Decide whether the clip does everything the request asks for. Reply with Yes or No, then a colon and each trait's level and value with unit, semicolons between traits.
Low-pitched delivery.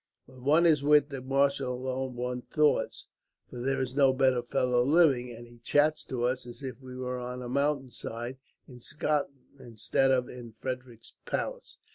Yes: low, 130 Hz